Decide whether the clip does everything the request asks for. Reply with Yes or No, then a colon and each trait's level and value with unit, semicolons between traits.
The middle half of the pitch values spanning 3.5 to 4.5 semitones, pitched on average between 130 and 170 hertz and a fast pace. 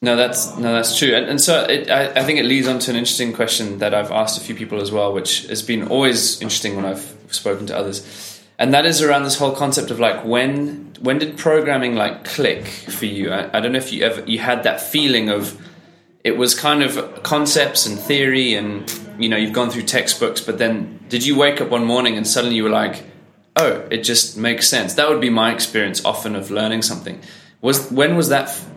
No: average, 3.8 semitones; low, 120 Hz; fast, 235 wpm